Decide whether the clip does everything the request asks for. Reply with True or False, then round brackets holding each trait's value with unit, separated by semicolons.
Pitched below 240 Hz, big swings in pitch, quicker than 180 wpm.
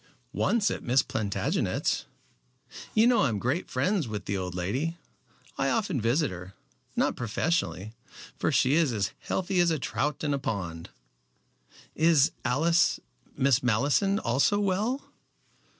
False (140 Hz; 7.8 semitones; 140 wpm)